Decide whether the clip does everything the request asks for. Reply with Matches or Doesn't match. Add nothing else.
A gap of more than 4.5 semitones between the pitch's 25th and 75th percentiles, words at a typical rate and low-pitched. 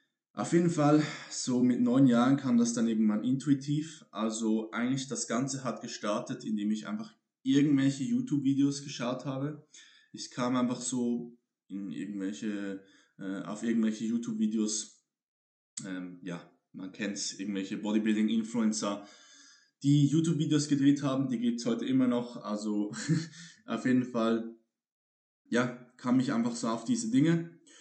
Matches